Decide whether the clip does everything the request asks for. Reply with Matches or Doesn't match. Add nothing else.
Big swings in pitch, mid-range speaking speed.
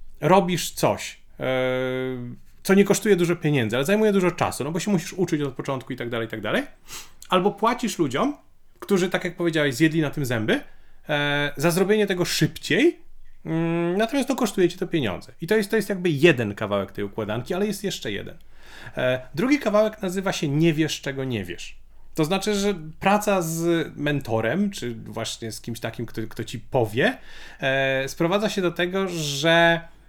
Doesn't match